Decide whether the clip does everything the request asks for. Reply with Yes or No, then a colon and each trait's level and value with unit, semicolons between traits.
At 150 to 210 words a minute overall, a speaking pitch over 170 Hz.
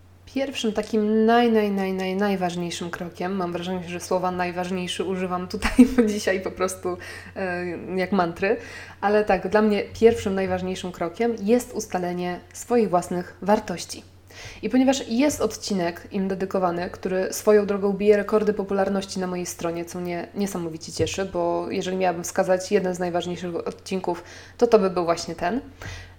Yes: average, 155 wpm; medium, 185 Hz